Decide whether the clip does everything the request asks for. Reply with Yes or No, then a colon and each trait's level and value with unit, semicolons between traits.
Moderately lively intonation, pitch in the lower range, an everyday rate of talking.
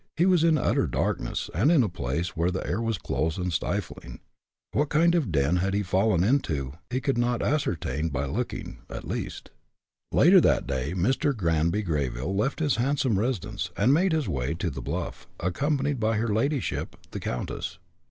No: wide, 8.6 semitones; low, 105 Hz; average, 185 wpm